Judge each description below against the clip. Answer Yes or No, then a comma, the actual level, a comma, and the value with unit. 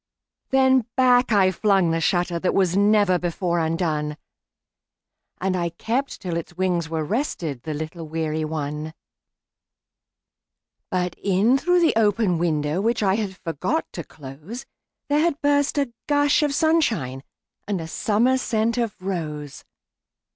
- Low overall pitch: No, medium, 185 Hz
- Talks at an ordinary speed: No, slow, 120 wpm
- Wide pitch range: Yes, wide, 6.6 semitones